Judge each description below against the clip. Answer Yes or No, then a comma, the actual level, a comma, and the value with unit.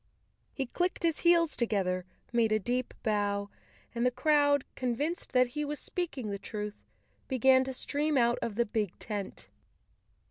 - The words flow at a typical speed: Yes, average, 155 wpm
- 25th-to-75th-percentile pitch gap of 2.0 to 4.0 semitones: No, average, 5.3 semitones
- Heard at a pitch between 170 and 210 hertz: No, high, 245 Hz